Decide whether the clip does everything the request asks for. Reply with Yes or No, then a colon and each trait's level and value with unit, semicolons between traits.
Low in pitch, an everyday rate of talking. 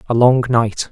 Yes: low, 120 Hz; average, 195 wpm